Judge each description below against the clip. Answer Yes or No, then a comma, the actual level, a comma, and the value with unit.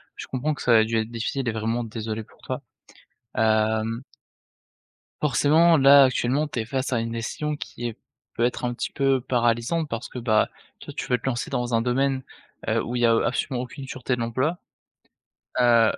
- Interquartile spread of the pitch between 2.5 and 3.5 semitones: Yes, average, 2.8 semitones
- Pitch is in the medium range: No, low, 120 Hz